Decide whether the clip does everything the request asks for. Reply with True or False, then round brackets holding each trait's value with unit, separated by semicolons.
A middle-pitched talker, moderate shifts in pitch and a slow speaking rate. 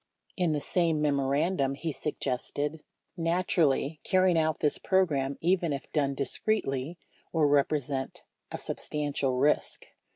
True (150 Hz; 3.3 semitones; 125 wpm)